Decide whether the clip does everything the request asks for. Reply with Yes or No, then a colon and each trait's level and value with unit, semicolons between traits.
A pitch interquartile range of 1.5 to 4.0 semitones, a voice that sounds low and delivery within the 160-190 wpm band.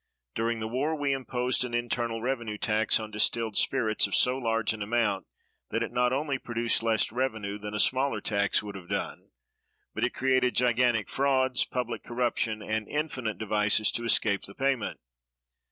Yes: average, 2.9 semitones; low, 115 Hz; average, 170 wpm